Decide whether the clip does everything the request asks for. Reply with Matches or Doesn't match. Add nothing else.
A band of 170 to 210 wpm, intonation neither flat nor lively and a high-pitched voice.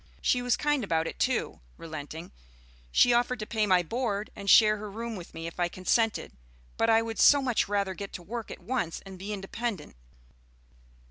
Matches